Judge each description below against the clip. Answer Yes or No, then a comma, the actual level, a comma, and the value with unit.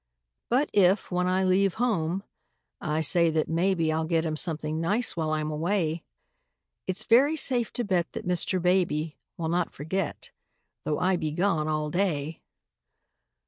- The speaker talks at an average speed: Yes, average, 155 wpm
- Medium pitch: Yes, medium, 175 Hz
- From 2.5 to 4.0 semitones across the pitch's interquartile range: Yes, average, 3.4 semitones